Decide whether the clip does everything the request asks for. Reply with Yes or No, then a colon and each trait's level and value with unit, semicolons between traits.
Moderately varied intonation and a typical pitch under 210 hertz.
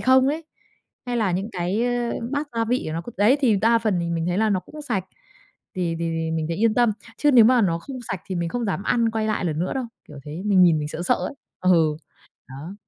No: wide, 5.7 semitones; high, 195 Hz